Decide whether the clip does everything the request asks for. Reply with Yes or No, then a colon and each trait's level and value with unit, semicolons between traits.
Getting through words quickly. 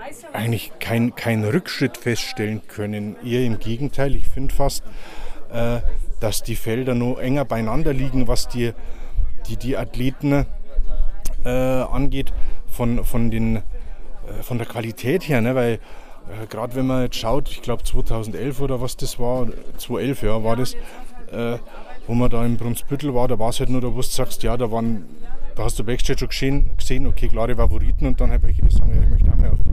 No: average, 180 wpm